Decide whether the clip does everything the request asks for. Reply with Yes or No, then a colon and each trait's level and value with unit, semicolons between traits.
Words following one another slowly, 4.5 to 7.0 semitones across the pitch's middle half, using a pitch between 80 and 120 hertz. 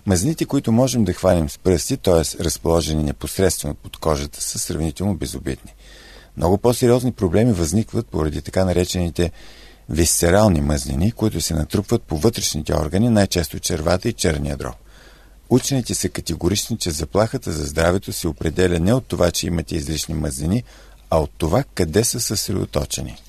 No: average, 145 wpm; average, 5.1 semitones; very low, 90 Hz